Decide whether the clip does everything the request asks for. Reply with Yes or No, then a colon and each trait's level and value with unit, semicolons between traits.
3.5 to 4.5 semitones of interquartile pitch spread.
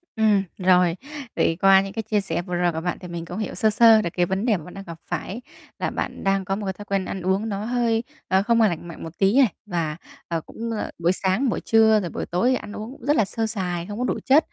Yes: average, 3.8 semitones